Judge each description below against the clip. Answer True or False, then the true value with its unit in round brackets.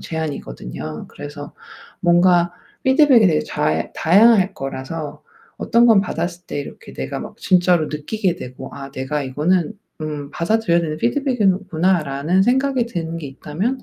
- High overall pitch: False (170 Hz)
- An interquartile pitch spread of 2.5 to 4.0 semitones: False (5.4 semitones)